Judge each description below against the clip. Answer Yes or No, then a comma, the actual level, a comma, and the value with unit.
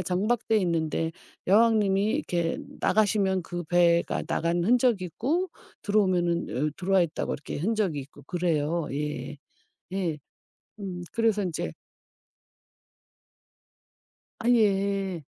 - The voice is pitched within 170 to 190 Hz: Yes, medium, 185 Hz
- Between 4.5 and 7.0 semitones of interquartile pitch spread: No, average, 3.7 semitones